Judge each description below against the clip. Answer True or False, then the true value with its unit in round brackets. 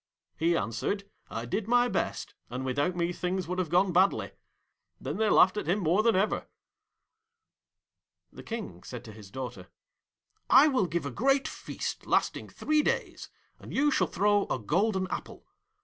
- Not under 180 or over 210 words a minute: False (165 wpm)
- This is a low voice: False (185 Hz)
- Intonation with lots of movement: True (6.8 semitones)